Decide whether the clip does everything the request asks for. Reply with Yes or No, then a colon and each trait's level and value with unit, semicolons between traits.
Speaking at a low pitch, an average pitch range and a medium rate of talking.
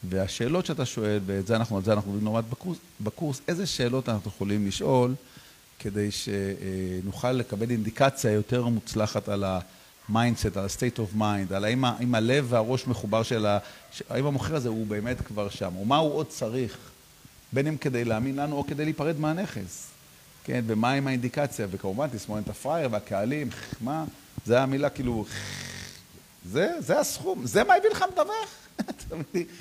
No: low, 120 Hz; average, 4.8 semitones; fast, 160 wpm